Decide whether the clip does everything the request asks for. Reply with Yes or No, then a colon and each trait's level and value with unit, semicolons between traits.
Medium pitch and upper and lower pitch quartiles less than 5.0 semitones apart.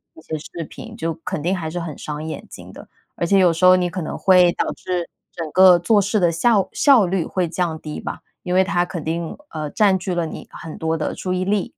Yes: medium, 175 Hz; narrow, 2.5 semitones